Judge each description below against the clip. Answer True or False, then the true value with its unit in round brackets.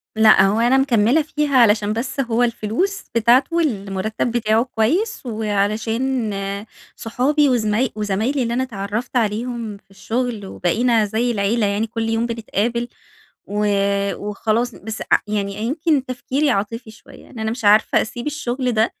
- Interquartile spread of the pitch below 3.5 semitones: True (3.0 semitones)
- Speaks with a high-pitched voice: True (230 Hz)